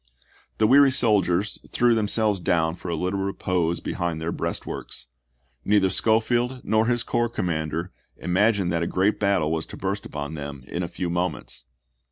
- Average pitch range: Yes, average, 4.4 semitones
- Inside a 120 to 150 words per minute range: No, average, 185 wpm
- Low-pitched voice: Yes, very low, 95 Hz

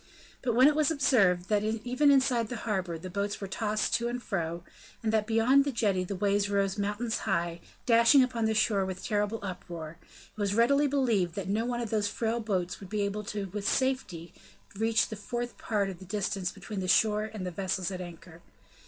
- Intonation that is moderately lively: Yes, average, 3.6 semitones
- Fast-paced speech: Yes, fast, 215 wpm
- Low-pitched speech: No, high, 210 Hz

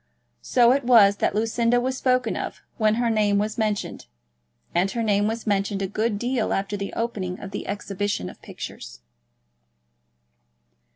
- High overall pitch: Yes, high, 215 Hz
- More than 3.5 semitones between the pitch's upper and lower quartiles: No, average, 2.7 semitones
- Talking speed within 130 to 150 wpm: No, average, 160 wpm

